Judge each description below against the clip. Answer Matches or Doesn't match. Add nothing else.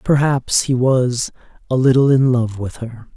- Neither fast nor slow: Matches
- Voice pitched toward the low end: Matches